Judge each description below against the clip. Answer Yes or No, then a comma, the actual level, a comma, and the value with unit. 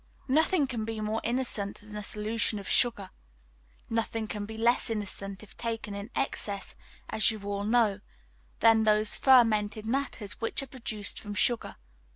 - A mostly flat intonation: Yes, narrow, 2.0 semitones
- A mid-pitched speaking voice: No, high, 220 Hz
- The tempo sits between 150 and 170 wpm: Yes, average, 160 wpm